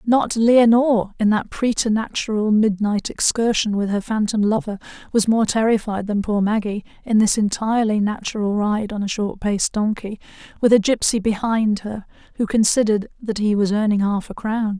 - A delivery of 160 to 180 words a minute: Yes, average, 165 wpm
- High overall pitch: Yes, high, 215 Hz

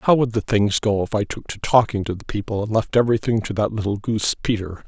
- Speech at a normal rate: No, fast, 260 wpm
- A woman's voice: No, male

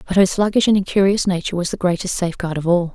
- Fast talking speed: Yes, fast, 245 wpm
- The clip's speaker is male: No, female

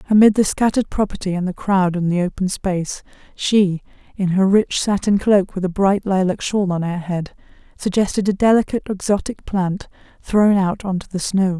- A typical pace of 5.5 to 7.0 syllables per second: No, 5.3 syllables/s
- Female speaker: Yes, female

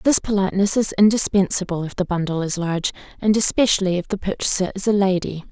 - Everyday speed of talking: Yes, average, 185 wpm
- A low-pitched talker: No, high, 190 Hz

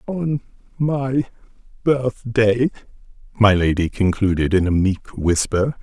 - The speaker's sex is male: Yes, male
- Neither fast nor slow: No, slow, 105 wpm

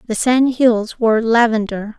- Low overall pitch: No, high, 230 Hz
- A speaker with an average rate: Yes, average, 150 wpm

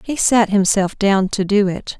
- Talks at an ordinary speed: No, fast, 210 wpm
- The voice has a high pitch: Yes, high, 200 Hz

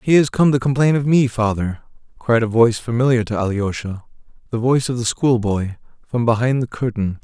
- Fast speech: No, average, 175 wpm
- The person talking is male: Yes, male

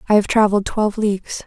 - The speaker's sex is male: No, female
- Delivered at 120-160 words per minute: No, fast, 205 wpm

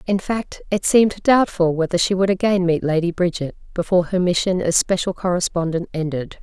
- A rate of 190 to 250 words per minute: No, average, 180 wpm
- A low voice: No, medium, 180 Hz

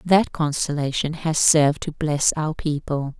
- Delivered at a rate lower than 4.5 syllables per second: Yes, 4.3 syllables/s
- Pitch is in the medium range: Yes, medium, 150 Hz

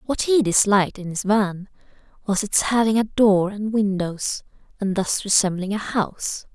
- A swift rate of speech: No, average, 165 wpm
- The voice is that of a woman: Yes, female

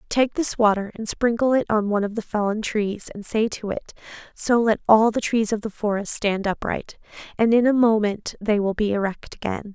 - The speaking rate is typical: No, fast, 215 wpm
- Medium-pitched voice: No, high, 215 Hz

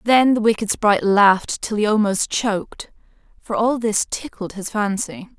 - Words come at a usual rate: Yes, average, 165 wpm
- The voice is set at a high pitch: Yes, high, 215 Hz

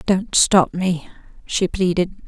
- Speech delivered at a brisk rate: No, slow, 130 wpm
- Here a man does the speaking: No, female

